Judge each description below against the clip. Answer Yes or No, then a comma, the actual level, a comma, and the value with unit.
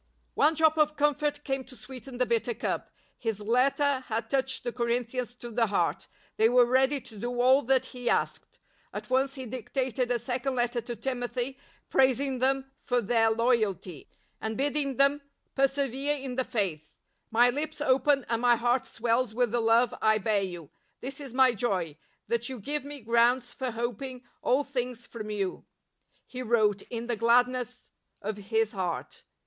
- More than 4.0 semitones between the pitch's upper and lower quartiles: No, average, 2.7 semitones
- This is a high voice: Yes, high, 245 Hz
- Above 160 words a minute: Yes, average, 180 wpm